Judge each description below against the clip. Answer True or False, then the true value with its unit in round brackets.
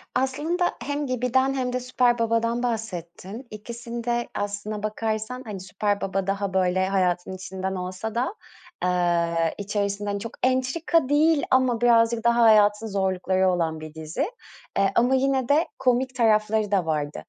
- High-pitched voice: True (220 Hz)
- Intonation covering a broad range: False (4.8 semitones)